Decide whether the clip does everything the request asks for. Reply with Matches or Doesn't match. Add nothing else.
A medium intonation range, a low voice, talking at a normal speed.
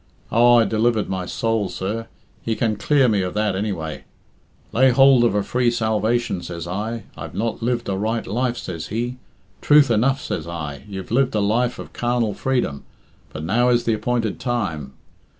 Matches